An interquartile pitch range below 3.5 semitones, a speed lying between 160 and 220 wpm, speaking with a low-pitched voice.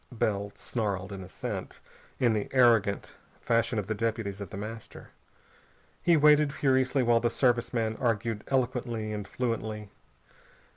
No: average, 2.8 semitones; average, 140 wpm; low, 115 Hz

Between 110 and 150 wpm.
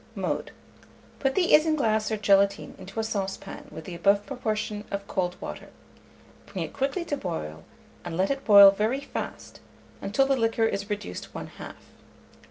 No: average, 165 wpm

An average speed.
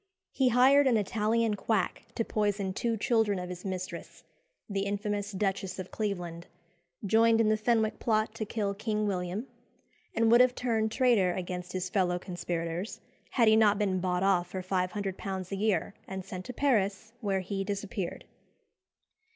Yes: average, 160 wpm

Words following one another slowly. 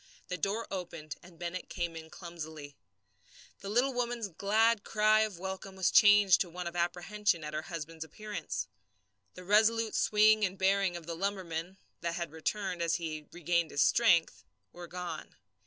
No: average, 165 wpm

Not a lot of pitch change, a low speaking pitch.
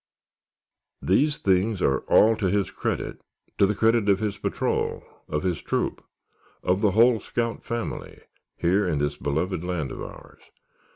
No: average, 3.9 semitones; low, 100 Hz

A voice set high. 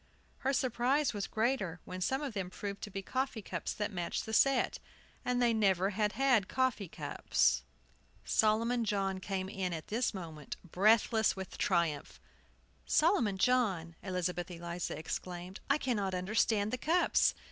Yes: high, 205 Hz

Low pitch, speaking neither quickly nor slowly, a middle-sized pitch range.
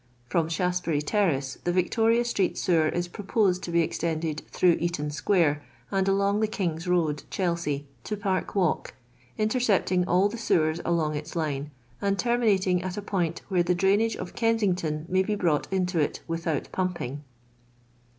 No: medium, 180 Hz; average, 160 wpm; average, 3.5 semitones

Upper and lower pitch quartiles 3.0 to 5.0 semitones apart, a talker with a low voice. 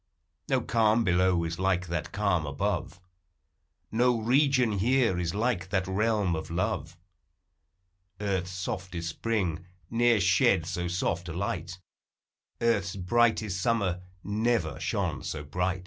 Yes: average, 4.2 semitones; very low, 95 Hz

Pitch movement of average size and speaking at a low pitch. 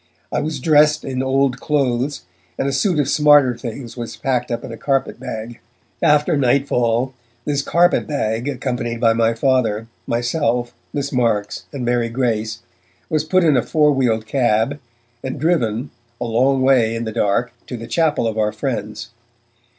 Yes: average, 3.6 semitones; low, 125 Hz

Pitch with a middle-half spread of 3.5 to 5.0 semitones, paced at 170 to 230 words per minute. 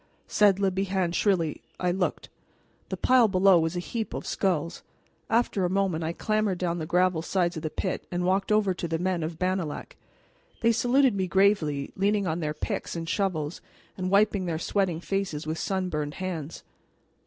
No: average, 3.0 semitones; average, 180 wpm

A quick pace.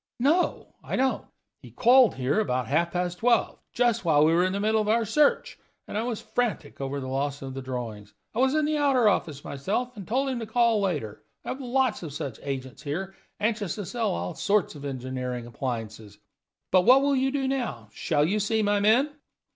Yes: fast, 210 wpm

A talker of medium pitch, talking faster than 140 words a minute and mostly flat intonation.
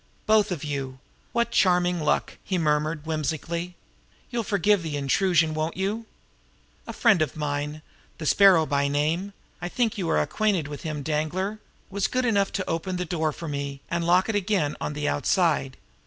No: medium, 165 Hz; average, 175 wpm; average, 4.6 semitones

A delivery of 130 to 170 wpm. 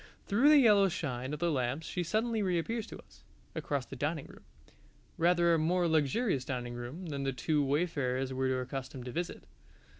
No: average, 180 wpm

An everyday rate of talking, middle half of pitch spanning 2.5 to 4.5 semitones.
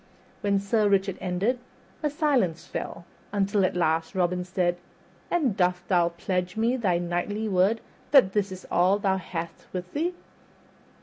Yes: average, 150 wpm; average, 3.1 semitones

